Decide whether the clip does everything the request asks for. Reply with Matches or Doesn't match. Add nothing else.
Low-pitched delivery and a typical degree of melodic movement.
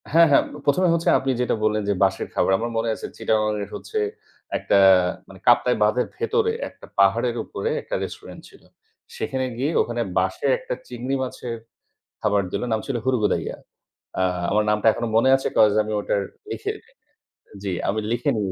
Matches